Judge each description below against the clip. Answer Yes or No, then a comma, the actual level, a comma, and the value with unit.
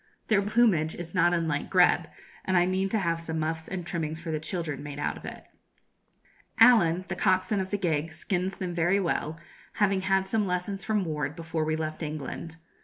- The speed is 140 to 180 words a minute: No, average, 195 wpm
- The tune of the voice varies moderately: Yes, average, 3.2 semitones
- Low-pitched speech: No, medium, 175 Hz